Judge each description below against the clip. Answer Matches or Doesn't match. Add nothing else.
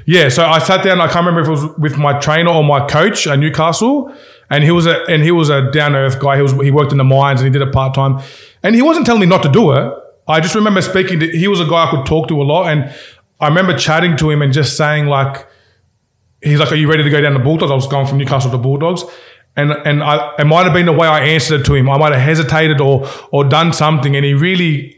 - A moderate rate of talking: Doesn't match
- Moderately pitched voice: Matches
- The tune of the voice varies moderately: Matches